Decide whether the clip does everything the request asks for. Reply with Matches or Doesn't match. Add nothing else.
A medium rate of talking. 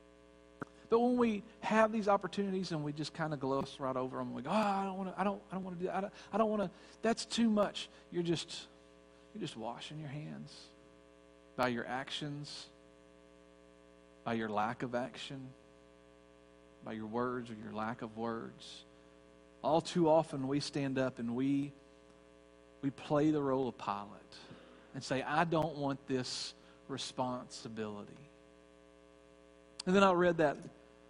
Matches